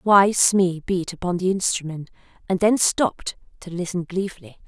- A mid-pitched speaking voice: Yes, medium, 180 Hz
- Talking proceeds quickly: No, average, 155 wpm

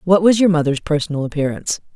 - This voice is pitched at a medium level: Yes, medium, 165 Hz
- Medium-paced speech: Yes, average, 185 wpm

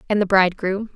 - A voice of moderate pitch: No, high, 195 Hz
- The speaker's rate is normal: Yes, average, 190 wpm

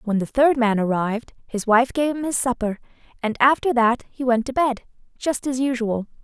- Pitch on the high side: Yes, high, 245 Hz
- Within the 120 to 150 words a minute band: No, average, 200 wpm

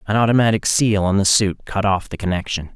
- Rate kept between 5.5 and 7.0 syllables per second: Yes, 5.8 syllables/s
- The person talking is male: Yes, male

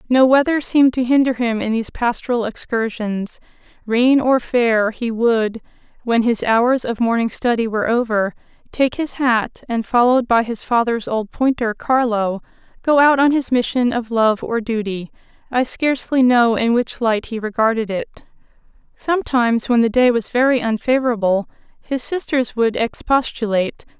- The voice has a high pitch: Yes, high, 235 Hz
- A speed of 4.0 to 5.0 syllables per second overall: Yes, 4.8 syllables/s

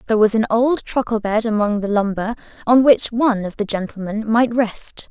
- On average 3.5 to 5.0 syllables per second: No, 5.3 syllables/s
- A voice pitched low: No, high, 220 Hz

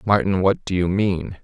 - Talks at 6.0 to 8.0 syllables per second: No, 4.5 syllables/s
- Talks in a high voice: No, very low, 95 Hz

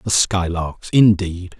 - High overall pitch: No, very low, 90 Hz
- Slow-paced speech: Yes, slow, 115 wpm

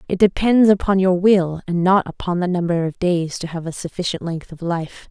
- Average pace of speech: No, fast, 225 wpm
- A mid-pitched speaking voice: Yes, medium, 180 Hz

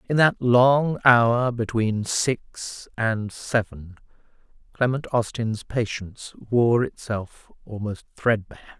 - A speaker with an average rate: No, slow, 100 wpm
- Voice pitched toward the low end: Yes, low, 115 Hz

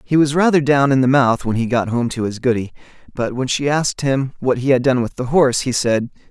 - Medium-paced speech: No, fast, 265 wpm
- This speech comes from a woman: No, male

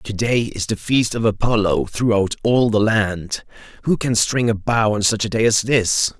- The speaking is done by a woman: No, male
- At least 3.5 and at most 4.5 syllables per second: Yes, 4.4 syllables/s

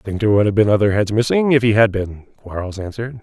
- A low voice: Yes, low, 105 Hz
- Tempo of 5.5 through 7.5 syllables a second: Yes, 6.8 syllables/s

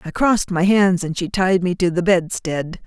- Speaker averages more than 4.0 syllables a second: Yes, 4.7 syllables/s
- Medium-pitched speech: Yes, medium, 180 Hz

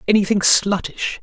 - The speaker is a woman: No, male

